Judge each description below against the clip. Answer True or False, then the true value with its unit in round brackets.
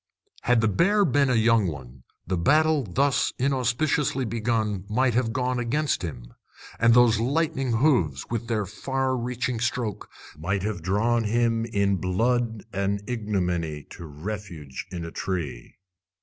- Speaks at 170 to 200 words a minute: False (145 wpm)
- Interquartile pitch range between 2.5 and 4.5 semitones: False (4.9 semitones)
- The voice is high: False (115 Hz)